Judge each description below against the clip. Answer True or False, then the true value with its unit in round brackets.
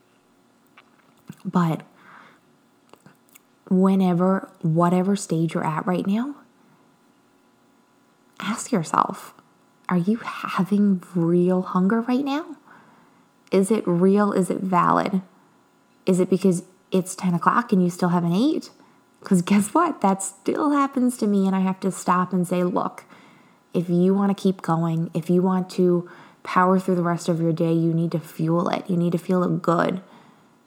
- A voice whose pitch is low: False (185 Hz)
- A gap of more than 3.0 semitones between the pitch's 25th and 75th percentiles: False (2.4 semitones)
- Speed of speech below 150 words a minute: False (155 wpm)